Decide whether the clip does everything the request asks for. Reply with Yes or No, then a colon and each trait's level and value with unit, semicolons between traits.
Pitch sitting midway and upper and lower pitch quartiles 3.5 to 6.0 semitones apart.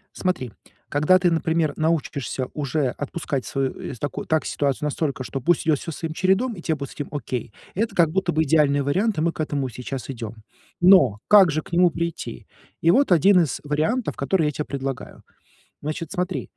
Yes: medium, 155 Hz; average, 3.9 semitones